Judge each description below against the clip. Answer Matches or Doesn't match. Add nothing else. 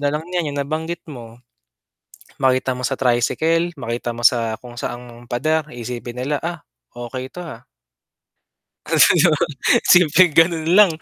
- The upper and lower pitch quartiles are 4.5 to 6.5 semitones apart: Matches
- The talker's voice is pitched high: Doesn't match